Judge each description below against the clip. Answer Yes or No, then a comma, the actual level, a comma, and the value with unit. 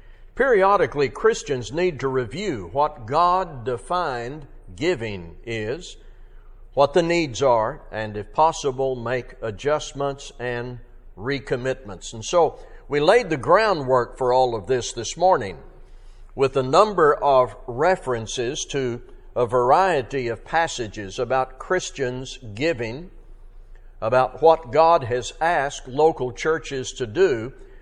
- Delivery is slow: Yes, slow, 120 wpm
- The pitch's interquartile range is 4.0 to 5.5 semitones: Yes, average, 5.1 semitones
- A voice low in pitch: Yes, low, 130 Hz